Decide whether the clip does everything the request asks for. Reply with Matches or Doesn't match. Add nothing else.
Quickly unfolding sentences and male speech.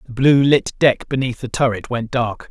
Matches